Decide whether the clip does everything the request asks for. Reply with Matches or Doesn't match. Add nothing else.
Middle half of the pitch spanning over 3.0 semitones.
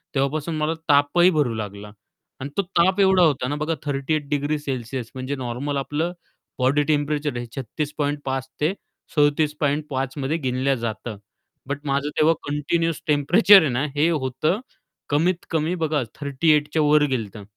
Doesn't match